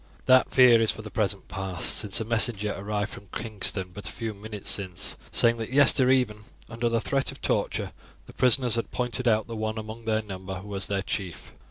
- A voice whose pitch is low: Yes, low, 110 Hz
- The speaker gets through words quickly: Yes, fast, 210 wpm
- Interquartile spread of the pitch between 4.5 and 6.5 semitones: No, average, 2.7 semitones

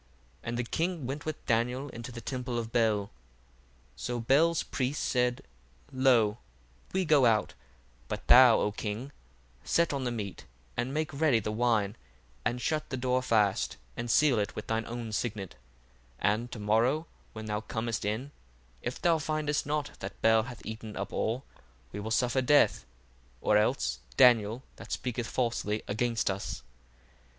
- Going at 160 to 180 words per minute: Yes, average, 165 wpm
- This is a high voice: No, low, 120 Hz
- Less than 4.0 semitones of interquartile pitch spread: Yes, average, 3.3 semitones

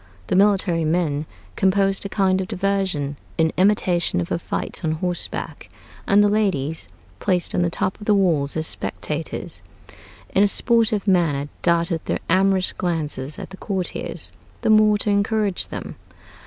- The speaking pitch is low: No, medium, 185 Hz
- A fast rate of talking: No, average, 155 wpm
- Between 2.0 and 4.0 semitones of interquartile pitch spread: Yes, average, 3.6 semitones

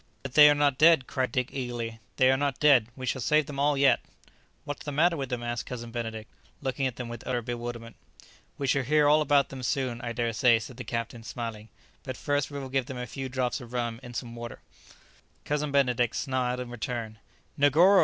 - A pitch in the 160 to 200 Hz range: No, low, 125 Hz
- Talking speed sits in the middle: No, fast, 220 wpm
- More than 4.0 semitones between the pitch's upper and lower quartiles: No, average, 2.9 semitones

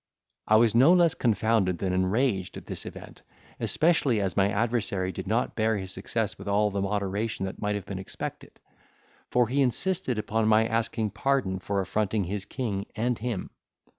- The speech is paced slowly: No, average, 175 wpm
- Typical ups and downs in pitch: Yes, average, 3.3 semitones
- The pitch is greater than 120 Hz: No, low, 110 Hz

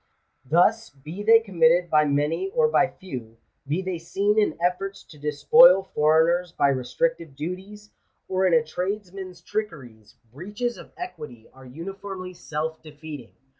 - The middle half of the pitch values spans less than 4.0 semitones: No, average, 4.7 semitones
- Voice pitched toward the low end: No, medium, 175 Hz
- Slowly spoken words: No, average, 150 wpm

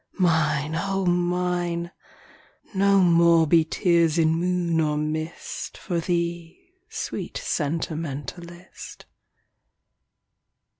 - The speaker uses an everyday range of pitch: No, narrow, 1.7 semitones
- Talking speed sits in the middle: No, slow, 85 wpm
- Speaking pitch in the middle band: Yes, medium, 170 Hz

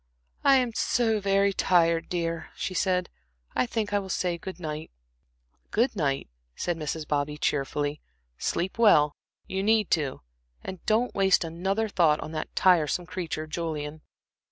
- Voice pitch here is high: No, medium, 175 Hz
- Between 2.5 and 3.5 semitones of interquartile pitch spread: No, average, 4.3 semitones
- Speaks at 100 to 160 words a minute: Yes, average, 150 wpm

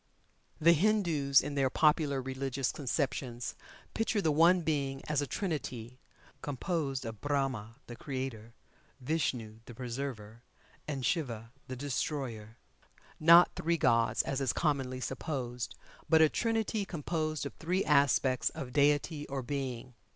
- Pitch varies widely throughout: No, average, 3.8 semitones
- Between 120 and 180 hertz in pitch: Yes, medium, 140 Hz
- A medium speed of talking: No, slow, 130 wpm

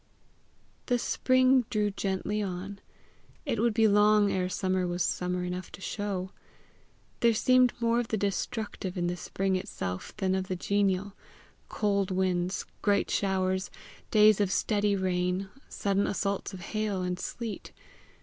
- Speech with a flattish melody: Yes, narrow, 2.3 semitones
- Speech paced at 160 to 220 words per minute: No, average, 145 wpm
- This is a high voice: Yes, high, 195 Hz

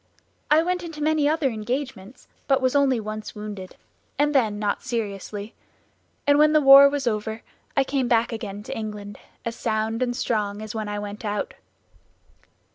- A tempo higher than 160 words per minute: Yes, average, 170 wpm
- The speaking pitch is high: Yes, high, 230 Hz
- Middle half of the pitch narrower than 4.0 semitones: No, average, 4.8 semitones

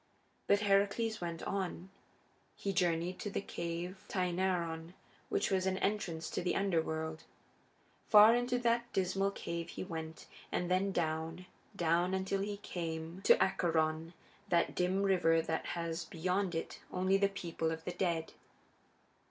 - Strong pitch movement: No, average, 2.9 semitones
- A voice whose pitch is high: No, medium, 180 Hz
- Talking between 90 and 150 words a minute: Yes, average, 145 wpm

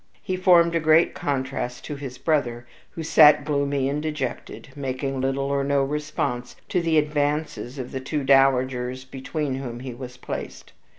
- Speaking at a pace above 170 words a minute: No, average, 165 wpm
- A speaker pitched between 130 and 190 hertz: Yes, medium, 140 Hz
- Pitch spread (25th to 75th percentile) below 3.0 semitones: Yes, narrow, 2.5 semitones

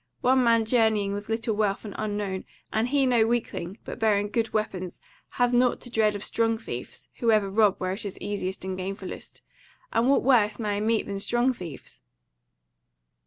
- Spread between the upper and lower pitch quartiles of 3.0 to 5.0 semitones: No, narrow, 2.6 semitones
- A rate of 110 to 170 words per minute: No, average, 185 wpm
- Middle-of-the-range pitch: No, high, 215 Hz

